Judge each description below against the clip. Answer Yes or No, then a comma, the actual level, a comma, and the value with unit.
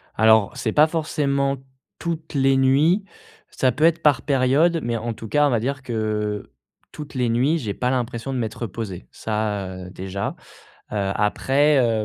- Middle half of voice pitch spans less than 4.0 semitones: No, average, 4.7 semitones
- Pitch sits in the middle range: No, low, 125 Hz